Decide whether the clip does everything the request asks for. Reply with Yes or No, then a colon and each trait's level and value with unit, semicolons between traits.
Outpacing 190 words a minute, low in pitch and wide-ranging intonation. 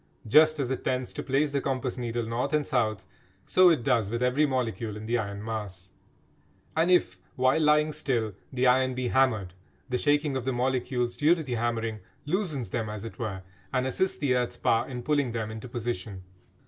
No: average, 200 wpm; low, 125 Hz; average, 3.7 semitones